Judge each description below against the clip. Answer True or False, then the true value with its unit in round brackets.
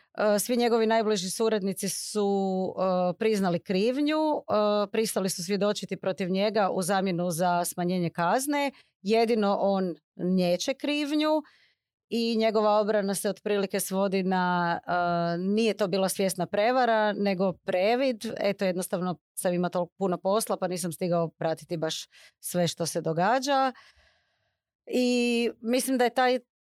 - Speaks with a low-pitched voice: False (200 Hz)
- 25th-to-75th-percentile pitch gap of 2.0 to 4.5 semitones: True (3.8 semitones)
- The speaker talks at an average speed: True (135 wpm)